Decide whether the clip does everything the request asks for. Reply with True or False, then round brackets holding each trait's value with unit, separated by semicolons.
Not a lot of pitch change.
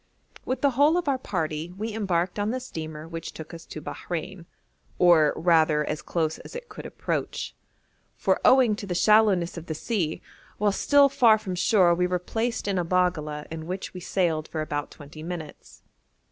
False (5.2 semitones)